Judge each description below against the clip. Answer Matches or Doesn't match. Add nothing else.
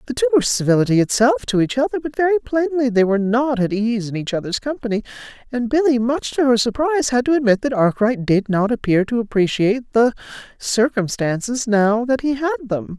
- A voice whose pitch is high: Matches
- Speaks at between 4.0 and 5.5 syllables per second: Doesn't match